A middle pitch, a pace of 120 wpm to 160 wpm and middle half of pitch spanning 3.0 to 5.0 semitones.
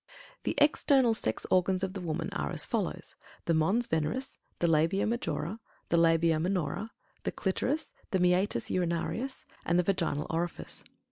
Yes: medium, 180 Hz; average, 150 wpm; average, 3.7 semitones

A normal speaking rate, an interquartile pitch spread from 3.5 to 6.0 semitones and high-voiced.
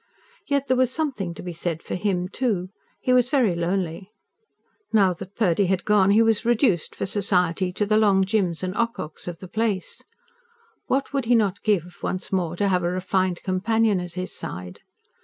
Yes: average, 190 wpm; average, 3.8 semitones; high, 195 Hz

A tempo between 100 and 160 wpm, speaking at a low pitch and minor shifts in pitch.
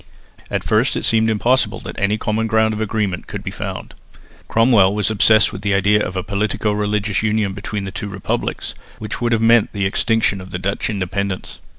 No: average, 195 wpm; low, 105 Hz; narrow, 2.0 semitones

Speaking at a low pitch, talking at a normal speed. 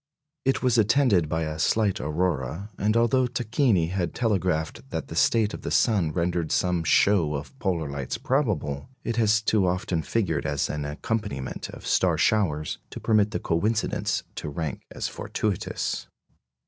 Yes: very low, 95 Hz; average, 160 wpm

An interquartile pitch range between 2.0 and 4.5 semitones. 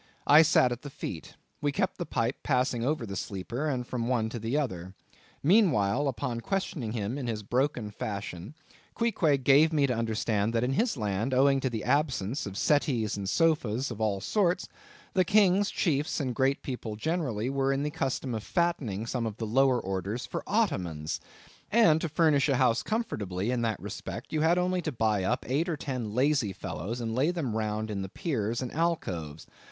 No: wide, 5.5 semitones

